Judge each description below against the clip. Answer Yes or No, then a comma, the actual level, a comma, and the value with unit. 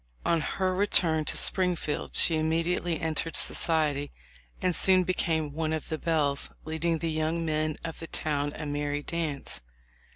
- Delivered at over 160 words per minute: No, average, 155 wpm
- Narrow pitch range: Yes, narrow, 1.8 semitones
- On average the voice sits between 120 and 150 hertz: No, medium, 160 Hz